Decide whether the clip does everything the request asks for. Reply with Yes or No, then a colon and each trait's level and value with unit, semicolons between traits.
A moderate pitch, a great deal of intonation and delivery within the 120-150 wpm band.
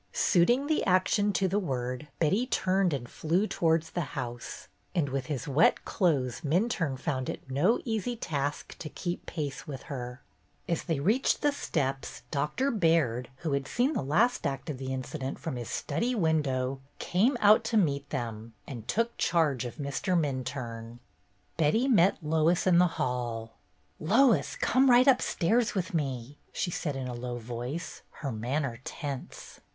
No: medium, 150 Hz; wide, 6.2 semitones; average, 165 wpm